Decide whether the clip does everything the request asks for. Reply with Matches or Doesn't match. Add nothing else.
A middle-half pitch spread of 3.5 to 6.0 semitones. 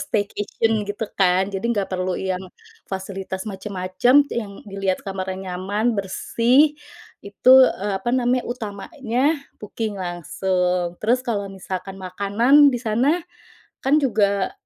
Matches